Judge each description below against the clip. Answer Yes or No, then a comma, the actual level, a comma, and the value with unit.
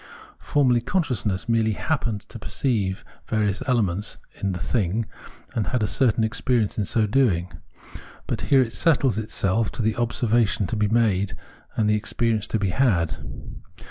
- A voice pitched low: Yes, low, 110 Hz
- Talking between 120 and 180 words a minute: Yes, average, 155 wpm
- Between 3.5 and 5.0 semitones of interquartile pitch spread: No, average, 2.9 semitones